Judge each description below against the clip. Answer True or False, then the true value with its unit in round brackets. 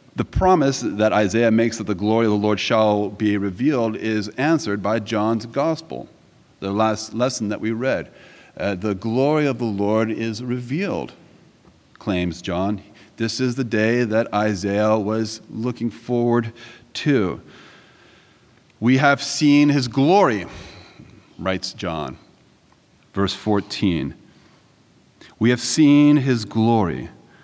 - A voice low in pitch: True (110 Hz)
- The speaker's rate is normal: False (130 wpm)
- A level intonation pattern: False (3.0 semitones)